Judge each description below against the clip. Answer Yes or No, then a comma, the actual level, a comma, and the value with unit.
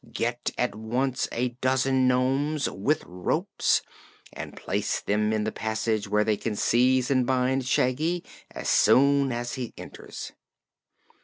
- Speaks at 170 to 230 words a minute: No, average, 140 wpm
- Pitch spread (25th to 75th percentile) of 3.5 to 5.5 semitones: No, average, 3.1 semitones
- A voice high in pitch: No, low, 125 Hz